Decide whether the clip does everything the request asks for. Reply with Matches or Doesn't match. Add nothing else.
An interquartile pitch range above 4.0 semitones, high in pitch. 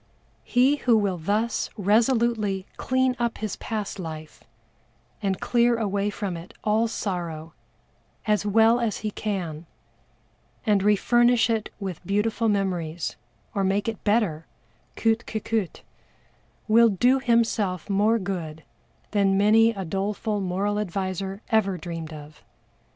Doesn't match